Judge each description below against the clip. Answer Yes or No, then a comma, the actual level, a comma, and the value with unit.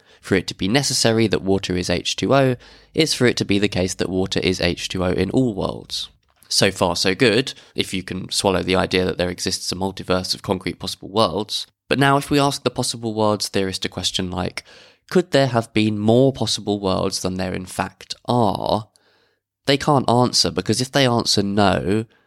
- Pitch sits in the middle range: No, low, 100 Hz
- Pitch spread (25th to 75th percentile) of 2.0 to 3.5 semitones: No, average, 4.6 semitones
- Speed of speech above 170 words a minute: Yes, average, 200 wpm